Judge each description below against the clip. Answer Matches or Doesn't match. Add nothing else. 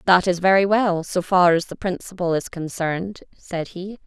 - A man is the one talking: Doesn't match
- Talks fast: Doesn't match